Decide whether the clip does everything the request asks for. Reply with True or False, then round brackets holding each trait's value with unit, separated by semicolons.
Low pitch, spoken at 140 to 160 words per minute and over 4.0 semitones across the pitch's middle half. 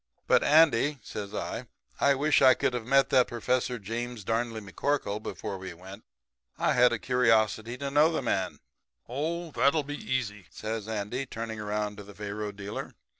False (115 Hz; 170 wpm; 4.5 semitones)